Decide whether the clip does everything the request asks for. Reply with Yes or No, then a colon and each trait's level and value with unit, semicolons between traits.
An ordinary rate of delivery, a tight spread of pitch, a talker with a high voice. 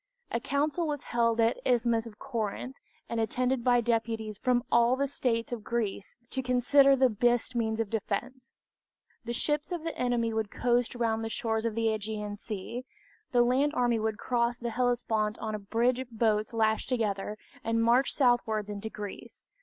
Yes: average, 185 wpm; narrow, 2.1 semitones; high, 235 Hz